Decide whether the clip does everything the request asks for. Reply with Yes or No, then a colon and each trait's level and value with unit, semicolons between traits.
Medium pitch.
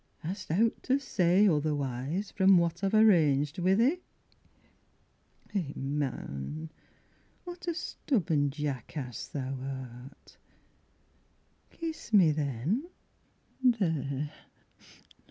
Yes: medium, 160 Hz